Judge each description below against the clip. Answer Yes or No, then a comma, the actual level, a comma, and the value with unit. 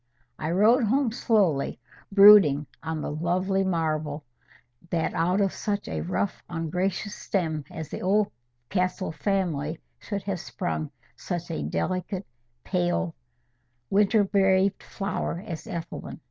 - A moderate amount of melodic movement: Yes, average, 3.7 semitones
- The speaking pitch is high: No, medium, 180 Hz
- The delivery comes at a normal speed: No, slow, 120 wpm